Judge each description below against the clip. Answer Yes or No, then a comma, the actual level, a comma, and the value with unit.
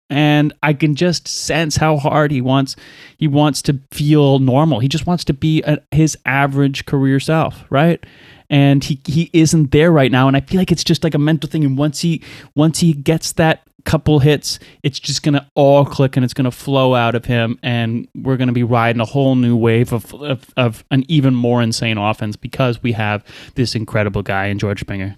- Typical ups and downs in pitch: Yes, average, 3.7 semitones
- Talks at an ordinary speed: No, fast, 210 wpm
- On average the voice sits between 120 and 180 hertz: Yes, medium, 140 Hz